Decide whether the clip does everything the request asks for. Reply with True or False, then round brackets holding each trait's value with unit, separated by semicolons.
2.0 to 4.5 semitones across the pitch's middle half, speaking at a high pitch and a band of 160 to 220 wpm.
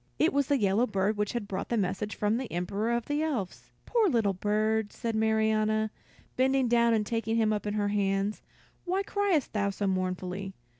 True (2.9 semitones; 215 Hz; 195 wpm)